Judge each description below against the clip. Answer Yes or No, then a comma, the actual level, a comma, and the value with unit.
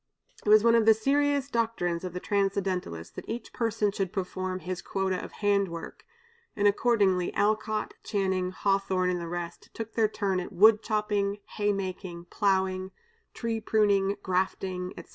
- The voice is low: No, high, 200 Hz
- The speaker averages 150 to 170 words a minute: Yes, average, 160 wpm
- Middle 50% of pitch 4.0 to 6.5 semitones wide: No, average, 2.7 semitones